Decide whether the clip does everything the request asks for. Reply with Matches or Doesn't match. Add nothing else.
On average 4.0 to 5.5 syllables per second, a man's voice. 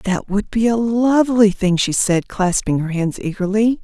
Doesn't match